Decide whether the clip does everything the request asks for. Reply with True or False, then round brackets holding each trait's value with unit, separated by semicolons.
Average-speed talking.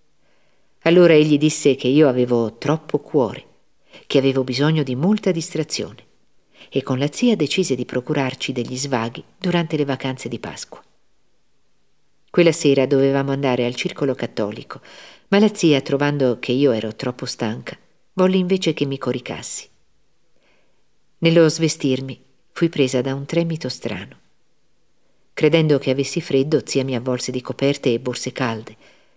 True (140 wpm)